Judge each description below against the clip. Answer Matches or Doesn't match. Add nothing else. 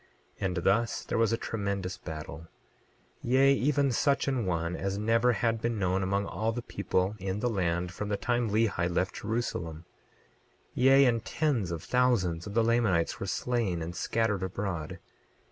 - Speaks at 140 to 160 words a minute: Doesn't match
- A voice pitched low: Matches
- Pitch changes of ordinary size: Matches